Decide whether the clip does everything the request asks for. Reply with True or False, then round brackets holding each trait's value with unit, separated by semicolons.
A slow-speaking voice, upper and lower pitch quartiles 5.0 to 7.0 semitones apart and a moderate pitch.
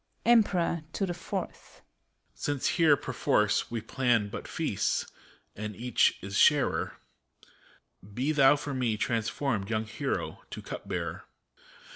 False (125 wpm; 5.3 semitones; 130 Hz)